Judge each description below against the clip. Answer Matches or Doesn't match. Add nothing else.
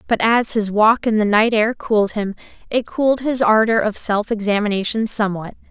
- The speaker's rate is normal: Matches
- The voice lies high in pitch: Matches